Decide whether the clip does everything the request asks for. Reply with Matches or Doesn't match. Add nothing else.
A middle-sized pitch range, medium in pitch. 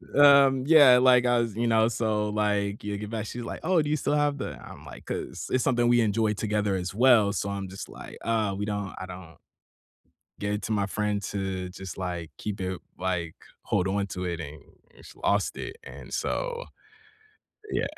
Doesn't match